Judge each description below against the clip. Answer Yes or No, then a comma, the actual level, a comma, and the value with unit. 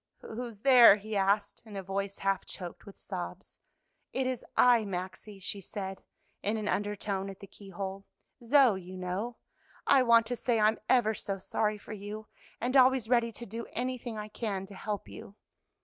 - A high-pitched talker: Yes, high, 210 Hz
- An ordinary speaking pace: Yes, average, 180 wpm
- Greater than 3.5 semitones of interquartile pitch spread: No, average, 3.0 semitones